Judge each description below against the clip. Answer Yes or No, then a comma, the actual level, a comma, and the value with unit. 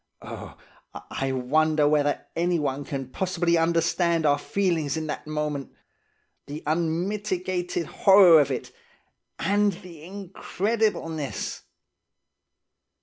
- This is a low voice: No, medium, 165 Hz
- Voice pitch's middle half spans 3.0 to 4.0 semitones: Yes, average, 3.6 semitones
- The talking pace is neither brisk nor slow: No, slow, 95 wpm